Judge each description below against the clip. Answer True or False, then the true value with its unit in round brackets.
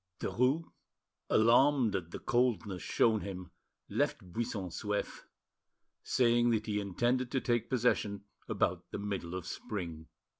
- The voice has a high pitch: False (110 Hz)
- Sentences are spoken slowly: True (125 wpm)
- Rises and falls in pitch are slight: False (4.2 semitones)